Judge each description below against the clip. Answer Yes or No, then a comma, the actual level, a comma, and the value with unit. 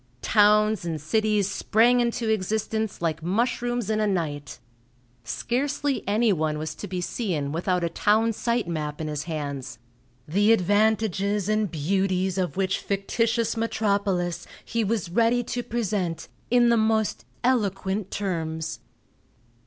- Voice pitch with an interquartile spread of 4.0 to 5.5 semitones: Yes, average, 4.5 semitones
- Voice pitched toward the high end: Yes, high, 205 Hz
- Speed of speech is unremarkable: No, slow, 130 wpm